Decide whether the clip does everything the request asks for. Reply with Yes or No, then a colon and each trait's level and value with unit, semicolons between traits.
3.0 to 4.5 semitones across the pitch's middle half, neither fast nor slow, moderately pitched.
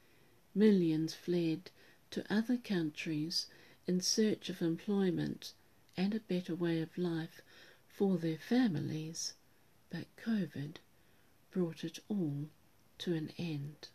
No: average, 3.3 semitones; slow, 110 wpm; medium, 170 Hz